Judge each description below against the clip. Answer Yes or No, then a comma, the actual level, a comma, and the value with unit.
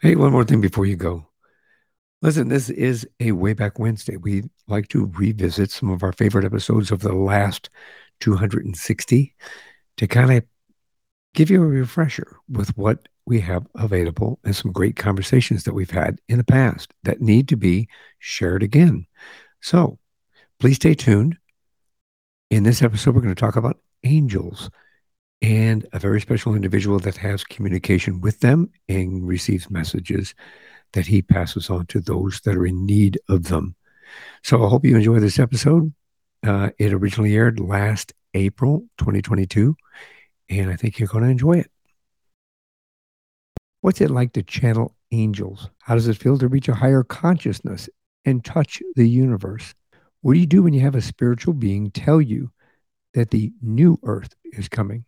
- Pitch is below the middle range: Yes, low, 110 Hz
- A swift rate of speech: No, average, 165 wpm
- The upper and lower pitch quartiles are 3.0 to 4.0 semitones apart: No, average, 4.5 semitones